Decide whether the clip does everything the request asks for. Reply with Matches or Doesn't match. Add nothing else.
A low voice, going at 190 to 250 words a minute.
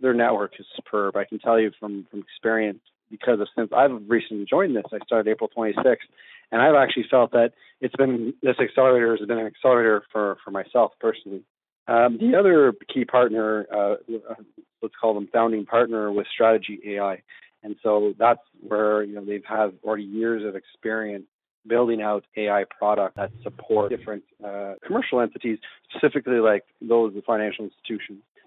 Doesn't match